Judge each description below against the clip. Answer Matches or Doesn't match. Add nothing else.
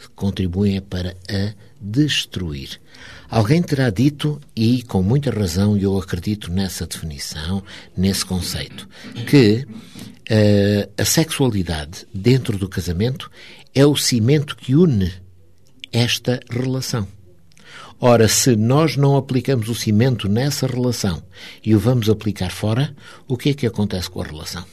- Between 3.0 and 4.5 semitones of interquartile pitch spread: Doesn't match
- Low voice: Matches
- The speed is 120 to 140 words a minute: Matches